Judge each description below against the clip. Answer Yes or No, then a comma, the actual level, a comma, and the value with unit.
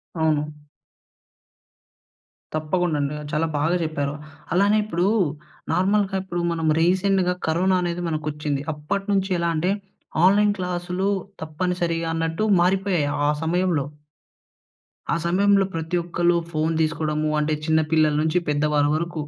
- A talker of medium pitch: Yes, medium, 170 Hz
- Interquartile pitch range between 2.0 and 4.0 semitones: Yes, average, 3.0 semitones